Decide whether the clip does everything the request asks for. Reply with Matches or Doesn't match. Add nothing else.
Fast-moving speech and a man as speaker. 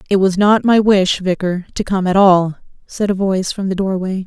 Doesn't match